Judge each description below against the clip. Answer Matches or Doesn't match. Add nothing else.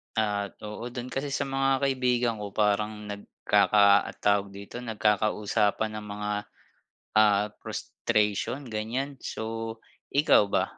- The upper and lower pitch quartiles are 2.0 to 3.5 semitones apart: Matches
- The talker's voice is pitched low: Matches